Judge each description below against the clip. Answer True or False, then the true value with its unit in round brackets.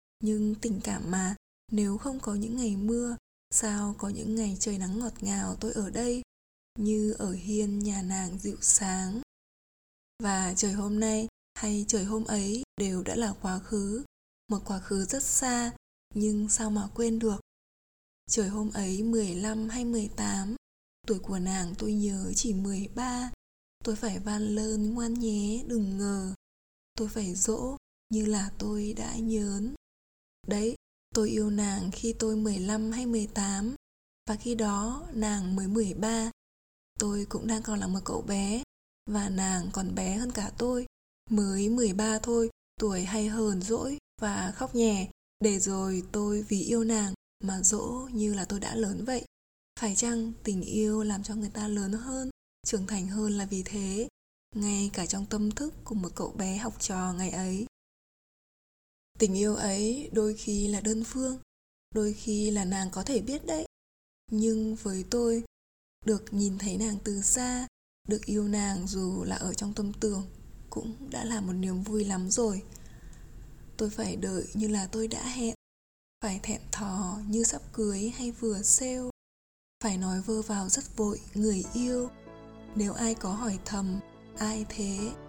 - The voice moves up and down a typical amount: False (2.1 semitones)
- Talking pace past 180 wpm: False (165 wpm)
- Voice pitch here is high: True (210 Hz)